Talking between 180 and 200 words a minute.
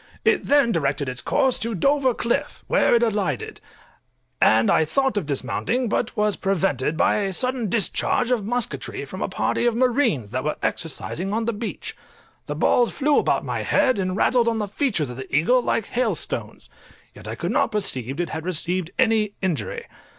Yes: average, 185 wpm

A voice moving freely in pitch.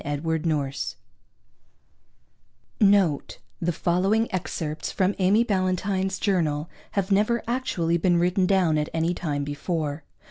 No: average, 3.6 semitones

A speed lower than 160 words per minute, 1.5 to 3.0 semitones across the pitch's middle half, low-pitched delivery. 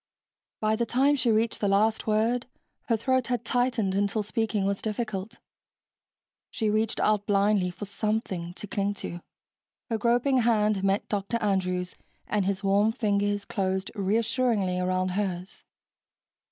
No: average, 140 wpm; narrow, 2.5 semitones; high, 210 Hz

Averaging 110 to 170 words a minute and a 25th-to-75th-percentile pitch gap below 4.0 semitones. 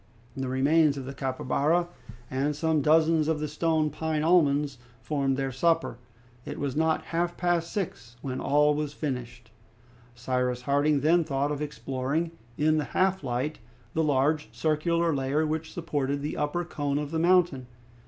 Yes: average, 160 wpm; average, 3.0 semitones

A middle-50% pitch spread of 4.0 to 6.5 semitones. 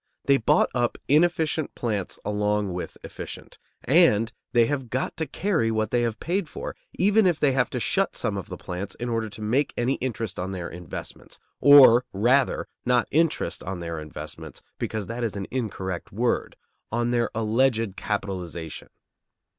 Yes: average, 4.8 semitones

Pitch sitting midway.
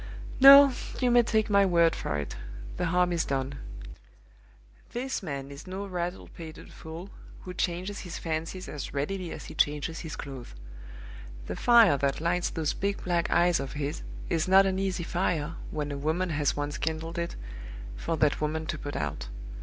Yes: medium, 165 Hz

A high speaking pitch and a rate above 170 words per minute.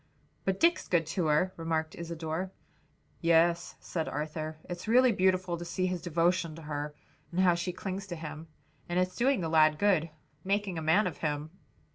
No: medium, 170 Hz; average, 180 wpm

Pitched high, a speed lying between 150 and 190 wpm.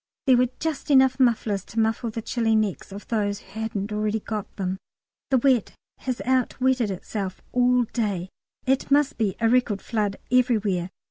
Yes: high, 225 Hz; average, 165 wpm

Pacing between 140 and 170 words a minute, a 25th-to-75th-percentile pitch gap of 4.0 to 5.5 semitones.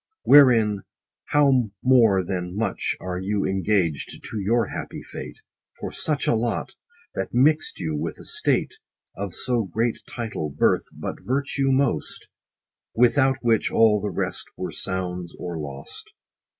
Yes: average, 145 wpm; average, 5.2 semitones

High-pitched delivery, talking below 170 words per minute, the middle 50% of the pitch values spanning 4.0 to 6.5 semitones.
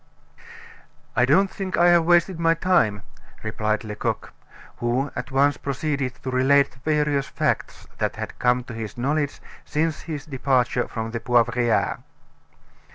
No: low, 135 Hz; average, 145 wpm; average, 4.3 semitones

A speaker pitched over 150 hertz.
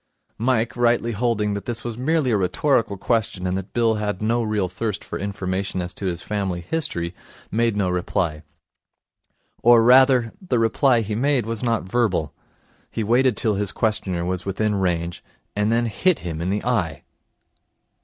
No: low, 105 Hz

